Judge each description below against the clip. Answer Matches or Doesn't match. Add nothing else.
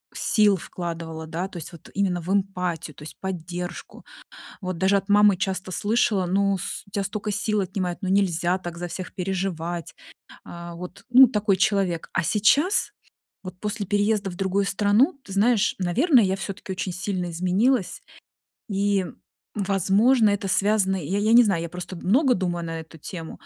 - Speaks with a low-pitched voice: Doesn't match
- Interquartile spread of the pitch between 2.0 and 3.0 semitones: Matches